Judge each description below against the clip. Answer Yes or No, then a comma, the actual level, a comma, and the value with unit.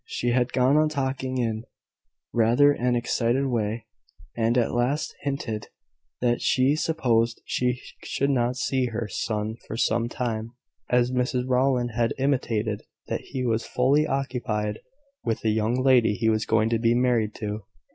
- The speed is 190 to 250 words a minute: No, average, 155 wpm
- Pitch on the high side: No, low, 120 Hz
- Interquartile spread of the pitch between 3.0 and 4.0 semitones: No, narrow, 2.4 semitones